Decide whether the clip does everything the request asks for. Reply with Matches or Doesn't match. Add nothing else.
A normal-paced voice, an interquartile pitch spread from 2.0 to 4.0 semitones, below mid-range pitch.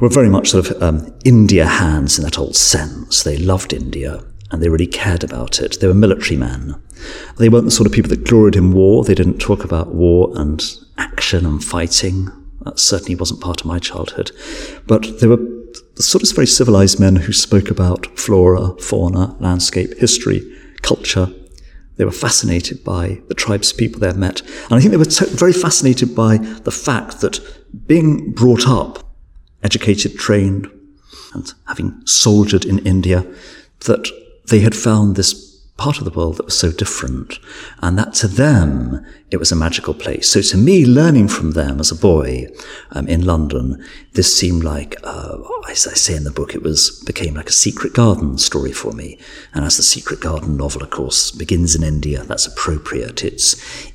Doesn't match